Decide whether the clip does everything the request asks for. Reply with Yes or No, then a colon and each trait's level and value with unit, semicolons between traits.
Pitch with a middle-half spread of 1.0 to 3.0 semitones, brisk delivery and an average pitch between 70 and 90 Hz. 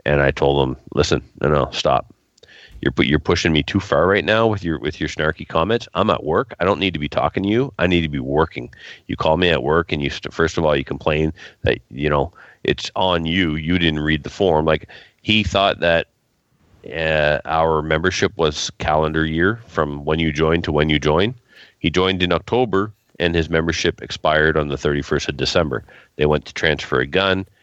No: average, 3.5 semitones; fast, 215 wpm; very low, 80 Hz